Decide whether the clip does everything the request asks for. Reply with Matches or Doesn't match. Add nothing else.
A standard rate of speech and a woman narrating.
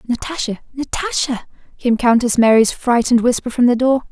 Matches